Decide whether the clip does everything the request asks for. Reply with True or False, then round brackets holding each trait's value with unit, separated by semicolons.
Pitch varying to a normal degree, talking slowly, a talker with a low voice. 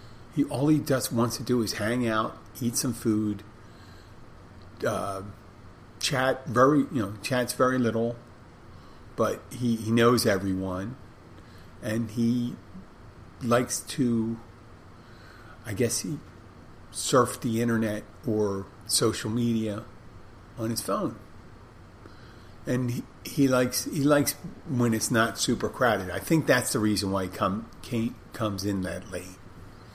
True (3.2 semitones; 130 wpm; 115 Hz)